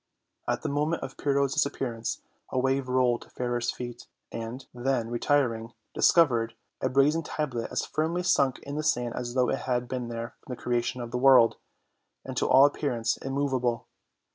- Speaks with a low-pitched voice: Yes, low, 125 Hz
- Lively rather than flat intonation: No, narrow, 2.6 semitones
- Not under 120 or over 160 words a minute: No, average, 180 wpm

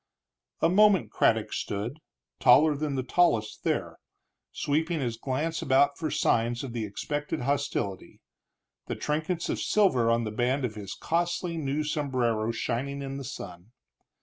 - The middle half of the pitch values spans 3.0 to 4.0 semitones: No, average, 4.7 semitones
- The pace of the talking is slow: No, average, 150 wpm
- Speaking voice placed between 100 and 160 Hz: Yes, low, 135 Hz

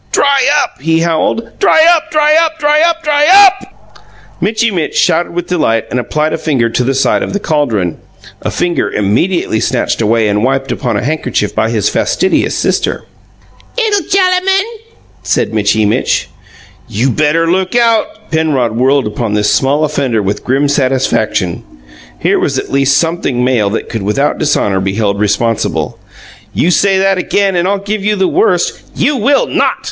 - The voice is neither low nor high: Yes, medium, 155 Hz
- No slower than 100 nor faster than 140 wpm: No, average, 175 wpm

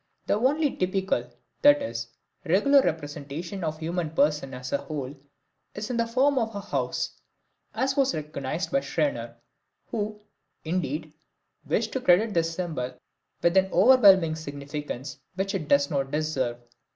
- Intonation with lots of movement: Yes, wide, 6.3 semitones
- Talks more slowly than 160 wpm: Yes, average, 150 wpm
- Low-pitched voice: No, medium, 170 Hz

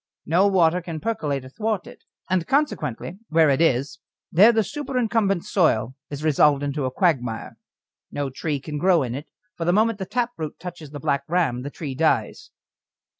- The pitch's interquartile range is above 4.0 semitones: Yes, wide, 5.4 semitones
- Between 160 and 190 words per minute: Yes, average, 175 wpm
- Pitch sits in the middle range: Yes, medium, 160 Hz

